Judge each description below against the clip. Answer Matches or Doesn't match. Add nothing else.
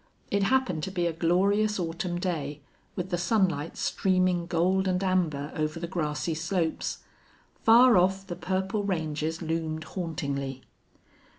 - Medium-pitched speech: Matches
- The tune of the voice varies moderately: Matches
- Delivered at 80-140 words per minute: Matches